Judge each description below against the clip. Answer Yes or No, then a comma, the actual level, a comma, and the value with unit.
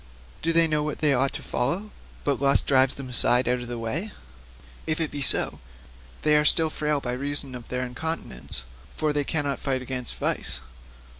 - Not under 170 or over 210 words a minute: Yes, average, 195 wpm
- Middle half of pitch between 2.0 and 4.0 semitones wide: Yes, average, 3.3 semitones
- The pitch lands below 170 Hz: Yes, medium, 140 Hz